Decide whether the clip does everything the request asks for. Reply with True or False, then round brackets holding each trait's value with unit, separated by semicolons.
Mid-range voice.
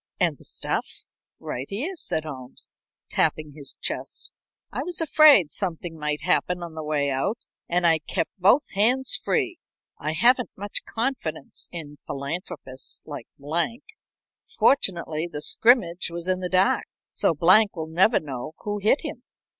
True (175 Hz)